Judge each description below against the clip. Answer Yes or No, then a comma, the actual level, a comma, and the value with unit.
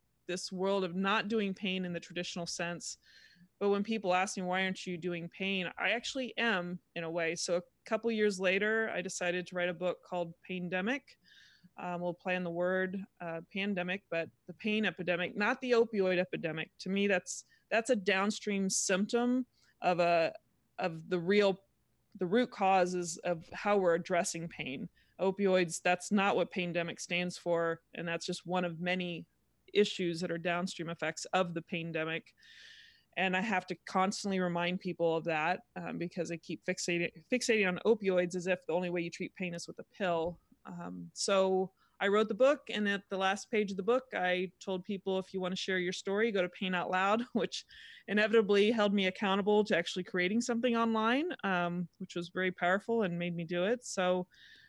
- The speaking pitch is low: No, medium, 185 Hz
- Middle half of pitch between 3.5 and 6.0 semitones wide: No, narrow, 2.6 semitones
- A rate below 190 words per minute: No, average, 195 wpm